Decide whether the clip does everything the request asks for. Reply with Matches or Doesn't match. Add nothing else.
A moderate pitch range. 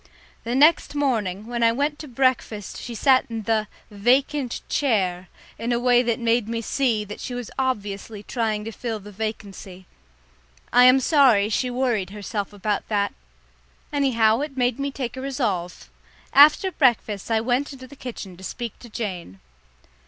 Matches